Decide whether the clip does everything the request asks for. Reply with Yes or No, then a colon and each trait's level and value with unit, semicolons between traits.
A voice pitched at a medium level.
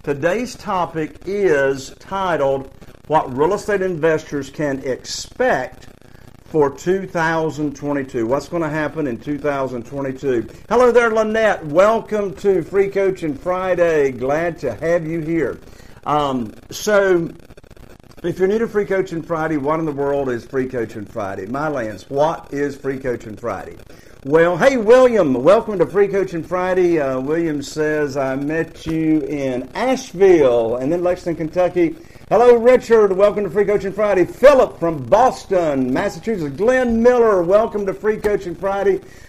Yes: medium, 165 Hz